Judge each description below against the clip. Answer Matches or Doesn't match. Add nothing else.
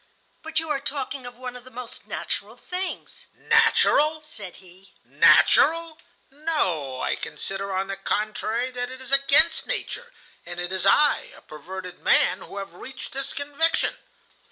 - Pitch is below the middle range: Doesn't match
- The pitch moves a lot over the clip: Matches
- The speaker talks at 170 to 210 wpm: Doesn't match